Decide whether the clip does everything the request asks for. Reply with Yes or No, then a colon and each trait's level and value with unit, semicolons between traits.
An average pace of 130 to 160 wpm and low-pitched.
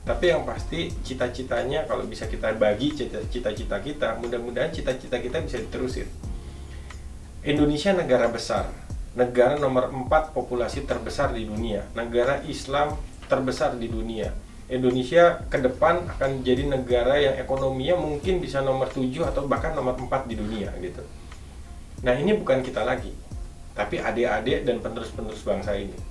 Yes: fast, 140 wpm; low, 125 Hz